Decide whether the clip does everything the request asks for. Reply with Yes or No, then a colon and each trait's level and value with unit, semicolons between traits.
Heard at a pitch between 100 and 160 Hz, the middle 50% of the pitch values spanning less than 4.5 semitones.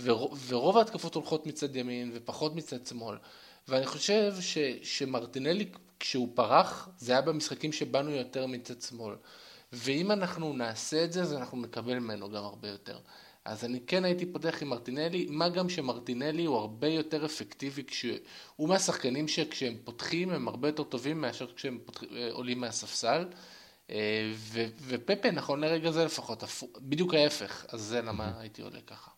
No: low, 135 Hz; average, 5.0 semitones